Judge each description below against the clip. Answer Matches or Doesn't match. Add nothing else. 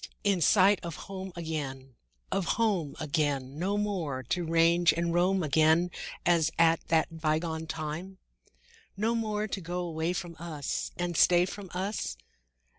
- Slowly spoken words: Doesn't match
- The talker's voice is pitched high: Doesn't match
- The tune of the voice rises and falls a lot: Doesn't match